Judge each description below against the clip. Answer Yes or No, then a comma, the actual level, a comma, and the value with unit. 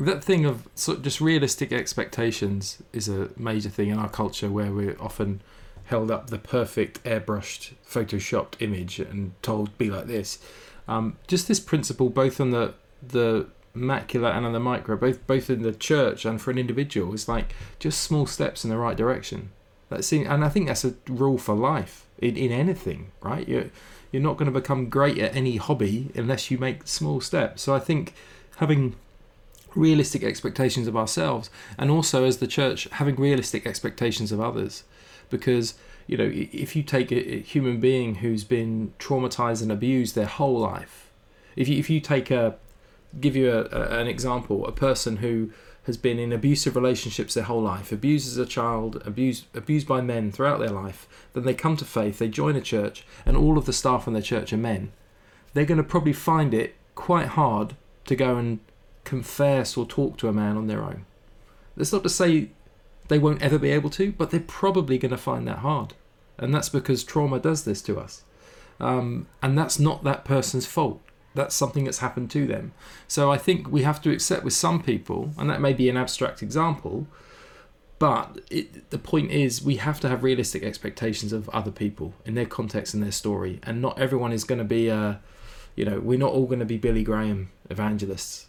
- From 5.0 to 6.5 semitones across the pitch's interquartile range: No, average, 4.2 semitones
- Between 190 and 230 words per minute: Yes, average, 200 wpm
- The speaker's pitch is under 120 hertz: No, low, 125 Hz